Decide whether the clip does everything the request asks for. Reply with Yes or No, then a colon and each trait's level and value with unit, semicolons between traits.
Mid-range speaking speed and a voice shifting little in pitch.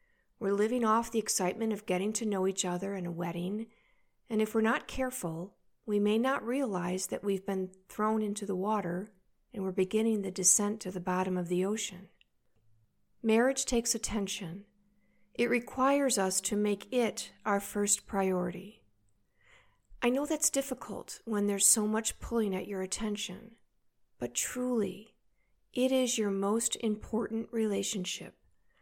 No: average, 150 wpm; average, 3.3 semitones